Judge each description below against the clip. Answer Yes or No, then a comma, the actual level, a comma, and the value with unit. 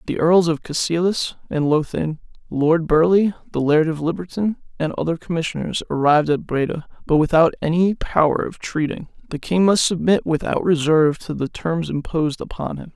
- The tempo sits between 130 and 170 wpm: Yes, average, 165 wpm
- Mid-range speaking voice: Yes, medium, 160 Hz